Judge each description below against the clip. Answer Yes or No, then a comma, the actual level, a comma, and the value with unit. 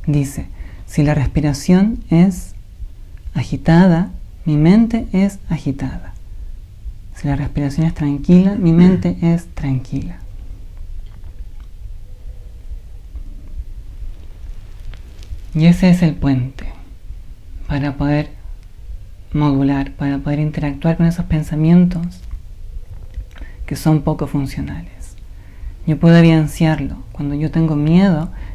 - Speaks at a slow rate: Yes, slow, 90 wpm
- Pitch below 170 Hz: Yes, medium, 140 Hz